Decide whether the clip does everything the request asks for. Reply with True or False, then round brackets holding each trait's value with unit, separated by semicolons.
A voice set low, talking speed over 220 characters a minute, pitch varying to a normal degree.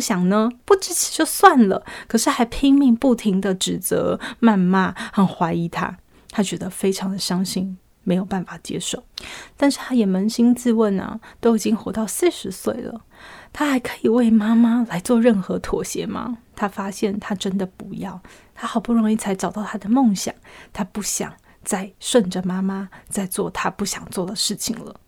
False (215 Hz; 260 characters per minute; 3.3 semitones)